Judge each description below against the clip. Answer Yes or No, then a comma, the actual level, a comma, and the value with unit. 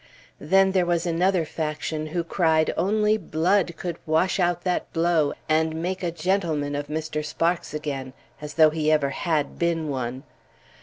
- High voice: No, medium, 160 Hz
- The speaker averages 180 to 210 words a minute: No, average, 160 wpm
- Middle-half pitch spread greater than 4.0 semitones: No, narrow, 2.5 semitones